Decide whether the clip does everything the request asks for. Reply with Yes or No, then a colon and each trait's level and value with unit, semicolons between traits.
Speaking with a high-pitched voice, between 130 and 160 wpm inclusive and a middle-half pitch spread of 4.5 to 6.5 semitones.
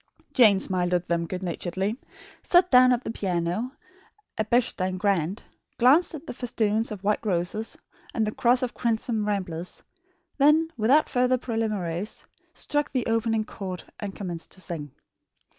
Yes: high, 215 Hz; average, 150 wpm; average, 5.0 semitones